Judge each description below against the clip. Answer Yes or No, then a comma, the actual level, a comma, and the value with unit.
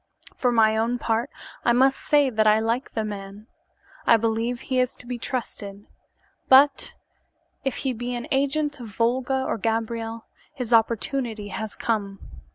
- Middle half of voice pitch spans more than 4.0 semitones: No, narrow, 2.6 semitones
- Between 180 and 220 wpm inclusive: No, average, 160 wpm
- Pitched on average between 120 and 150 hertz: No, high, 230 Hz